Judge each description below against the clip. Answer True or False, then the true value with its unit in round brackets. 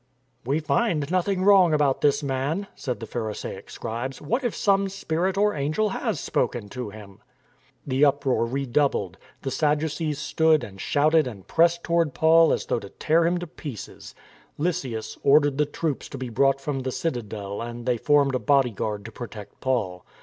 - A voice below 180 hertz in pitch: True (140 Hz)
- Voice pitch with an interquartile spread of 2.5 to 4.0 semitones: False (5.1 semitones)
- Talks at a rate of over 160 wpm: True (180 wpm)